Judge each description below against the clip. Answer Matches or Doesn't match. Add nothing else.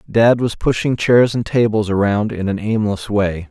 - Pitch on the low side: Matches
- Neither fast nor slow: Matches